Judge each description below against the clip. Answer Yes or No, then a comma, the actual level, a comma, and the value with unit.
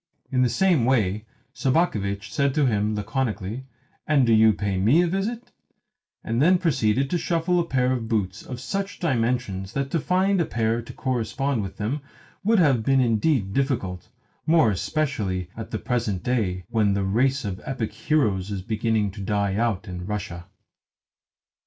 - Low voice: Yes, low, 115 Hz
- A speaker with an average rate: Yes, average, 170 wpm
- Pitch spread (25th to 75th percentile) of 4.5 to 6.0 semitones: Yes, average, 5.2 semitones